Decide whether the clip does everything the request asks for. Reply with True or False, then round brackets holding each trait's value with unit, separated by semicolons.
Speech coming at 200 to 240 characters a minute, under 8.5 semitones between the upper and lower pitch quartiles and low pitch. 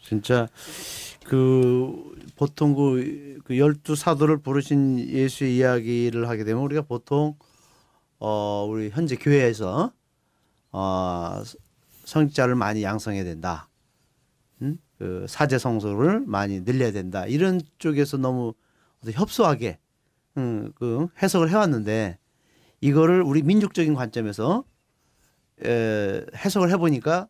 True (235 characters per minute; 5.7 semitones; 130 Hz)